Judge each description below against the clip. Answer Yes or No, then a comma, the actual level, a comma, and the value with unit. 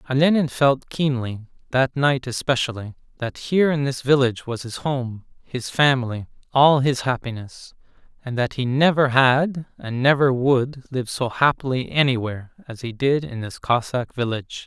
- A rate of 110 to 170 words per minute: Yes, average, 155 wpm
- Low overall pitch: Yes, low, 130 Hz